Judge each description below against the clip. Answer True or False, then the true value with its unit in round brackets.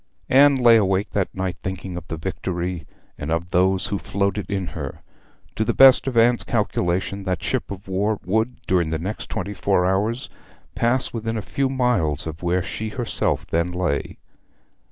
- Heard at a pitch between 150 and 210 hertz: False (95 Hz)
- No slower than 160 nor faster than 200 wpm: True (175 wpm)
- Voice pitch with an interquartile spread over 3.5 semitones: True (4.0 semitones)